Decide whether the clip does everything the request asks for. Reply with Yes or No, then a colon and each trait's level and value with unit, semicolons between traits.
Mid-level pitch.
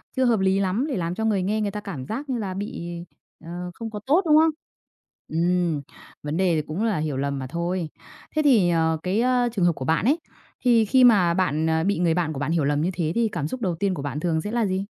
Yes: medium, 180 Hz